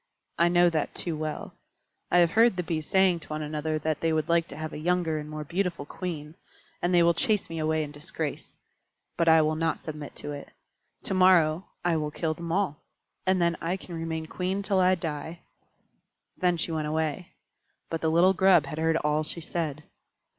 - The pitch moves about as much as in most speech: No, narrow, 2.3 semitones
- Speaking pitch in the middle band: Yes, medium, 165 Hz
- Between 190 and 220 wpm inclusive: Yes, fast, 205 wpm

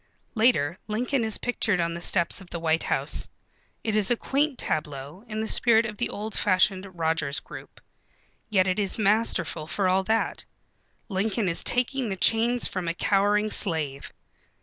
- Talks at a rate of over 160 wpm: Yes, average, 170 wpm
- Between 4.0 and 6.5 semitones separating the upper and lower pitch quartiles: Yes, average, 4.6 semitones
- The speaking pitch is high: Yes, high, 200 Hz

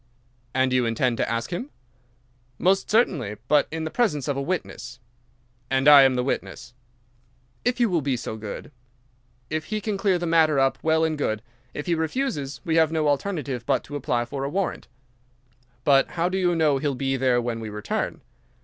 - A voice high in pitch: No, medium, 145 Hz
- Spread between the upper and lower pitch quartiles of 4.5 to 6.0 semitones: Yes, average, 4.8 semitones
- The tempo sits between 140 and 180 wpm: No, average, 190 wpm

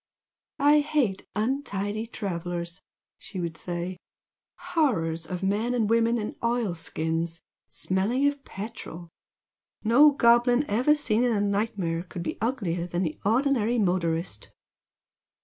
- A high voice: Yes, high, 205 Hz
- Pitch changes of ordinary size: No, wide, 5.7 semitones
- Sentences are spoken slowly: Yes, slow, 125 wpm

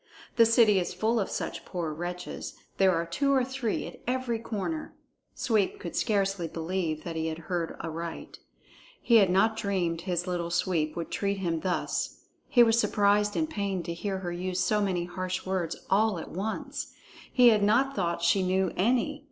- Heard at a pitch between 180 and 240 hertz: Yes, high, 190 Hz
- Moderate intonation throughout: Yes, average, 4.2 semitones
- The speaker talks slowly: No, average, 185 wpm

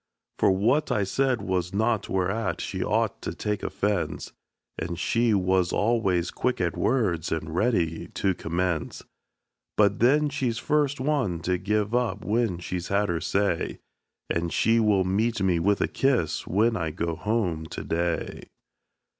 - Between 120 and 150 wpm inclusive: No, average, 160 wpm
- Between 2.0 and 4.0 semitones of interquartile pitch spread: No, average, 4.7 semitones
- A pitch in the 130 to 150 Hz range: No, low, 100 Hz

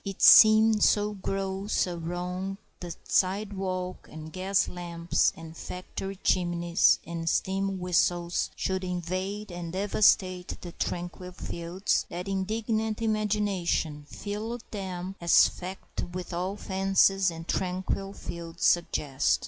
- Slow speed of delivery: Yes, slow, 120 wpm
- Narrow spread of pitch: Yes, narrow, 2.1 semitones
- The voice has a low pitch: No, medium, 185 Hz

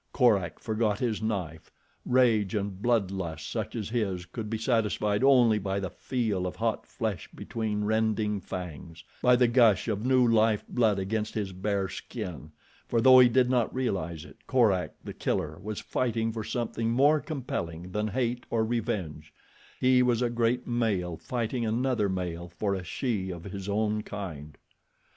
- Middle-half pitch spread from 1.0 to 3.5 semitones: No, average, 3.9 semitones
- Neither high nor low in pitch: No, low, 110 Hz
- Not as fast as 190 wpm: Yes, average, 160 wpm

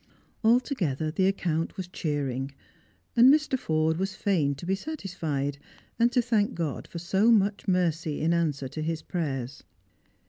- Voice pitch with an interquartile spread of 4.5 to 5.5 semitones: Yes, average, 5.2 semitones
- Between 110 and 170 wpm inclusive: Yes, average, 160 wpm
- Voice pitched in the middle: Yes, medium, 170 Hz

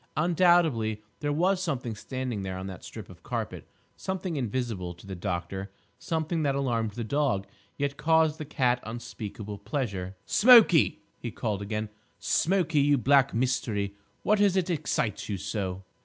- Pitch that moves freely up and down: Yes, wide, 7.2 semitones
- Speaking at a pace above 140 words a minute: Yes, average, 155 wpm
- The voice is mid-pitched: No, low, 125 Hz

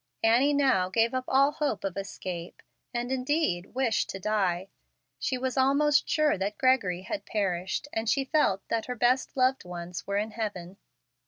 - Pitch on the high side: Yes, high, 225 Hz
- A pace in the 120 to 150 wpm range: No, average, 170 wpm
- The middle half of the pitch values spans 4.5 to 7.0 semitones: Yes, wide, 5.6 semitones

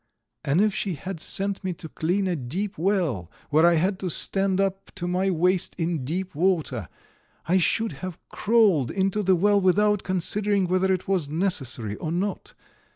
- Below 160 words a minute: No, average, 175 wpm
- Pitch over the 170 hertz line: Yes, medium, 185 Hz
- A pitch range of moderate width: Yes, average, 3.1 semitones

